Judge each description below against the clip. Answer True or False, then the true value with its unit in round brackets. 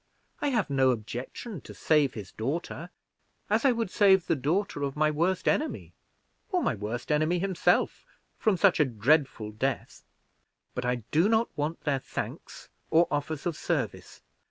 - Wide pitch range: True (6.0 semitones)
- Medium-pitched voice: True (155 Hz)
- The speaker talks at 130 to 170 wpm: True (160 wpm)